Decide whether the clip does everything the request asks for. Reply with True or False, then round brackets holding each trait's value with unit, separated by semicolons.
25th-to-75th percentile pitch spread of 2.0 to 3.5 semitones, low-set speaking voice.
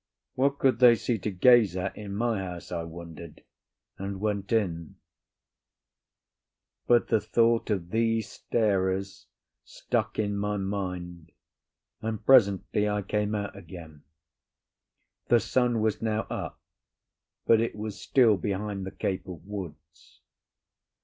True (3.2 semitones; 100 Hz)